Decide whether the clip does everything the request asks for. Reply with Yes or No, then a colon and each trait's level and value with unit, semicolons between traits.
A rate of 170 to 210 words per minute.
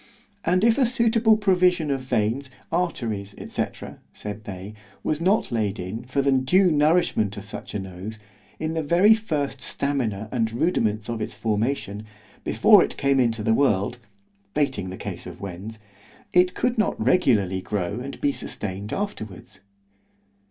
No: average, 155 wpm